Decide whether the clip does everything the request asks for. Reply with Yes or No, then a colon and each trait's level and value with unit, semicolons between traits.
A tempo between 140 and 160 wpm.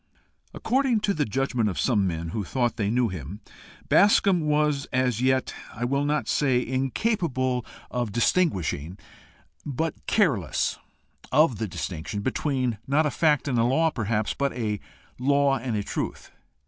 Yes: average, 150 wpm